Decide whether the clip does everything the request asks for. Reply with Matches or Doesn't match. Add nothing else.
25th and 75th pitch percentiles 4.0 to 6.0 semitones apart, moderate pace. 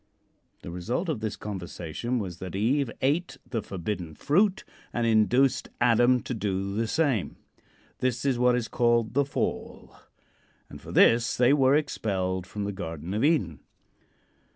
Matches